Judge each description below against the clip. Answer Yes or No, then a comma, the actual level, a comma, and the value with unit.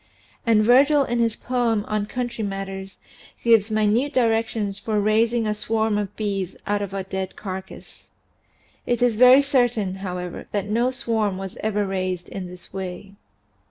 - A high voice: Yes, high, 210 Hz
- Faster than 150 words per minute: Yes, average, 160 wpm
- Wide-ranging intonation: No, average, 3.2 semitones